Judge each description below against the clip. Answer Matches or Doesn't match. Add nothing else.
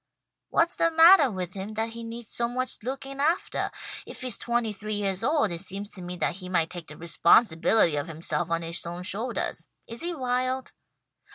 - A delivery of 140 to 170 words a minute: Doesn't match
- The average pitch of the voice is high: Matches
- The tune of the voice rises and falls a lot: Matches